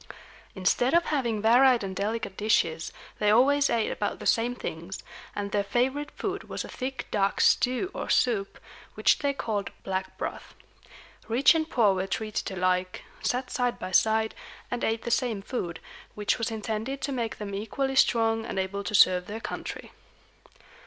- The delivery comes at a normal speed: Yes, average, 170 wpm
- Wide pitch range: No, average, 4.0 semitones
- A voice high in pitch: Yes, high, 220 Hz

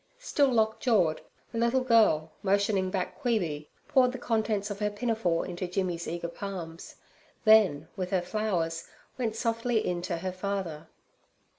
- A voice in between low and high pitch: No, high, 200 Hz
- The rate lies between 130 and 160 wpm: Yes, average, 150 wpm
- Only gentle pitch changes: No, average, 4.4 semitones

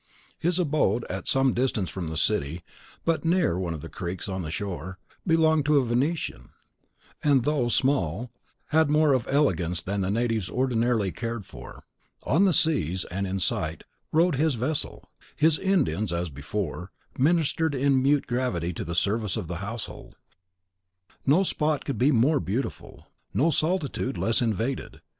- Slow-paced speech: No, average, 160 wpm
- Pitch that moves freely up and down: Yes, wide, 8.0 semitones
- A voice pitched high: No, low, 120 Hz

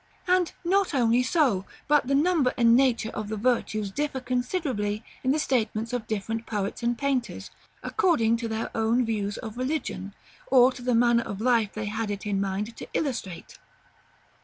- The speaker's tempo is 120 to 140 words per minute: No, average, 175 wpm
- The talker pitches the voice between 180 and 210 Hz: No, high, 235 Hz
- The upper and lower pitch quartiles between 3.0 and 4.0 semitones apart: Yes, average, 3.6 semitones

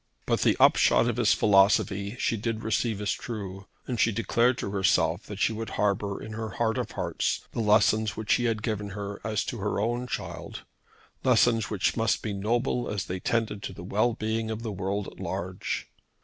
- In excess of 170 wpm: Yes, average, 200 wpm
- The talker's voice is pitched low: Yes, low, 110 Hz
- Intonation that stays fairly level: Yes, narrow, 2.1 semitones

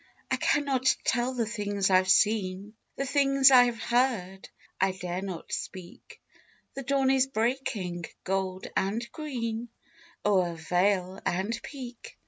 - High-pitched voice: Yes, high, 215 Hz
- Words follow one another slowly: Yes, slow, 130 wpm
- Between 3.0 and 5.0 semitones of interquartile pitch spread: No, wide, 5.5 semitones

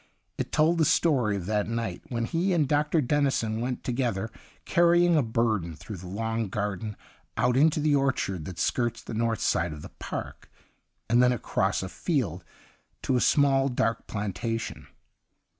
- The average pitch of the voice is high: No, low, 115 Hz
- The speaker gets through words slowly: No, average, 165 wpm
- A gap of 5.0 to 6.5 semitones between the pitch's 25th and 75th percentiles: Yes, average, 5.3 semitones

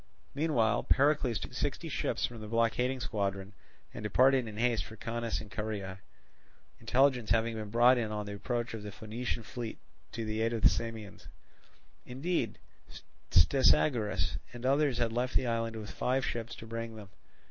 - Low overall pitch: Yes, low, 115 Hz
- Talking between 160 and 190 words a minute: Yes, average, 170 wpm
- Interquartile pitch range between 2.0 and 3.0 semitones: Yes, narrow, 2.4 semitones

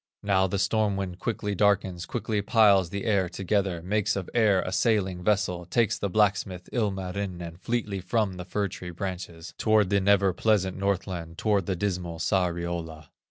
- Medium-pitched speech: No, very low, 95 Hz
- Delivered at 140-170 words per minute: Yes, average, 160 wpm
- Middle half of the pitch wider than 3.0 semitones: No, narrow, 2.4 semitones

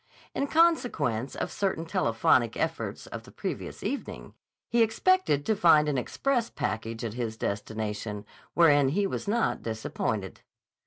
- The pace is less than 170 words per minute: Yes, average, 140 wpm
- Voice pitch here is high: No, medium, 145 Hz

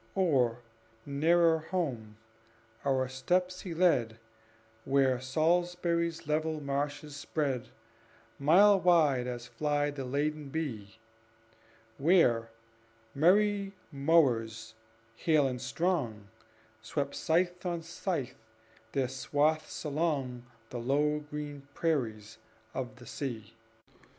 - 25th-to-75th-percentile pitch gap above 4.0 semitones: Yes, average, 4.5 semitones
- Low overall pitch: No, medium, 145 Hz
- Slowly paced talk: Yes, slow, 95 wpm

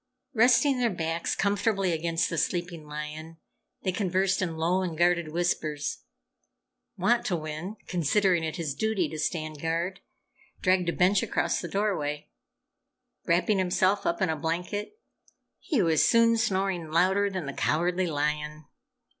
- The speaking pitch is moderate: Yes, medium, 175 Hz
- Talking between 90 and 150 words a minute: Yes, average, 140 wpm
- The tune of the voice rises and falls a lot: No, average, 3.4 semitones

